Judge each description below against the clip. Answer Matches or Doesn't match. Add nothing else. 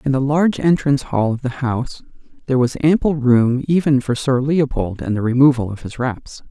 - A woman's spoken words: Doesn't match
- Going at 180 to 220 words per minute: Matches